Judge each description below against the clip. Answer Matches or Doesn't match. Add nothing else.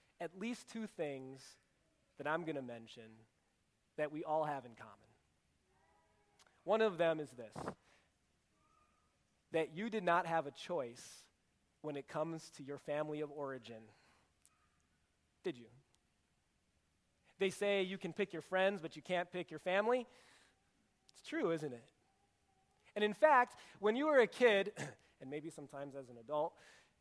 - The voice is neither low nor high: Matches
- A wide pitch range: Matches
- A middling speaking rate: Matches